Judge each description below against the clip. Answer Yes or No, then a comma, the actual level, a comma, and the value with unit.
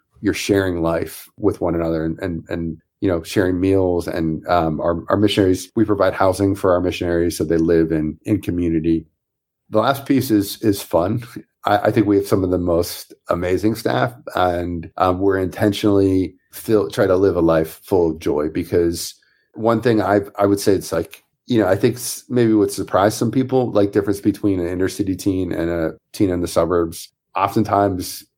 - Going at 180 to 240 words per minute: Yes, average, 195 wpm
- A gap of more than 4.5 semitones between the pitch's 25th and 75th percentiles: No, average, 3.3 semitones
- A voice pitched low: Yes, very low, 95 Hz